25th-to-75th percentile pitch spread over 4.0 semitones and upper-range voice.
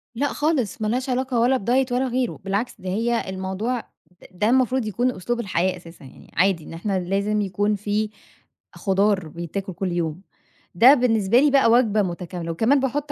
Yes: average, 4.9 semitones; high, 210 Hz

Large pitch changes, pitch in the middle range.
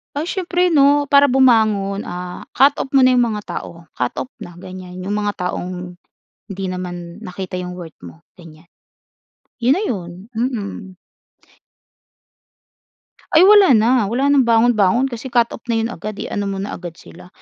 No: wide, 6.0 semitones; high, 210 Hz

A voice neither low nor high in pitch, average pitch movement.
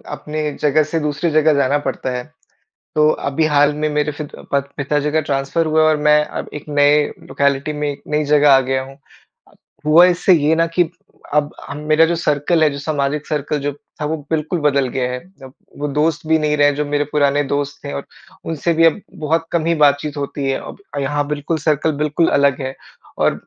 No: medium, 150 Hz; narrow, 1.6 semitones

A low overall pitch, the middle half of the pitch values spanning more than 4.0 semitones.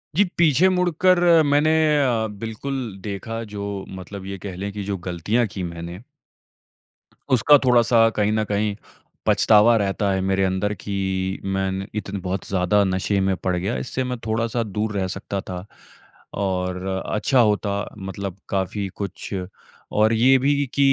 No: low, 100 Hz; average, 3.3 semitones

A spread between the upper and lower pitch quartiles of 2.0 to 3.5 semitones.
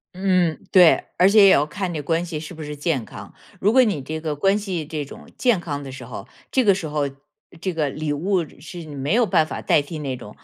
No: average, 4.3 semitones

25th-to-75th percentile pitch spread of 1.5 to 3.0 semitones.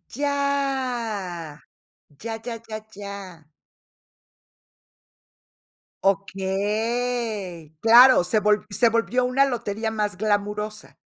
No: average, 3.5 semitones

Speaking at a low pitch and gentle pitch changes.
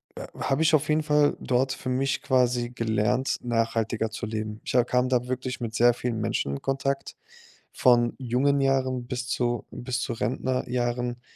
Yes: low, 125 Hz; narrow, 1.8 semitones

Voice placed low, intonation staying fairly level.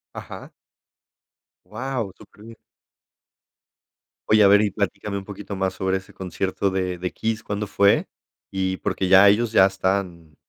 Yes: low, 100 Hz; narrow, 1.7 semitones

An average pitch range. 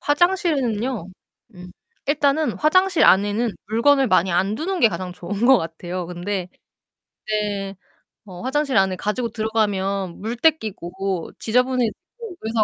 No: wide, 5.7 semitones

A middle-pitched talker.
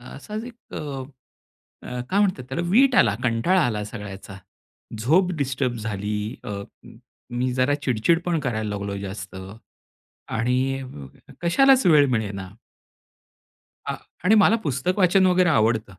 No: low, 130 Hz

